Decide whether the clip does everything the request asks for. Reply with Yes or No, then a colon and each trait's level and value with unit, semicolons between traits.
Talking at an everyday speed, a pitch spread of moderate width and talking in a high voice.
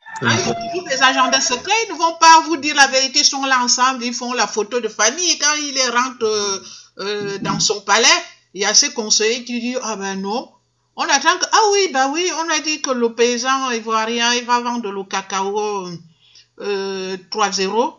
No: average, 210 wpm; wide, 5.9 semitones; high, 245 Hz